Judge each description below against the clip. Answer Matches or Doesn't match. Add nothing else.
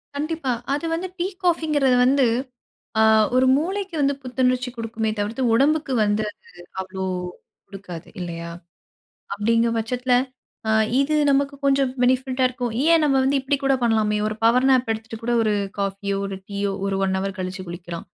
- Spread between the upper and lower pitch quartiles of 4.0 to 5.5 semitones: Matches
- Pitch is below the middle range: Doesn't match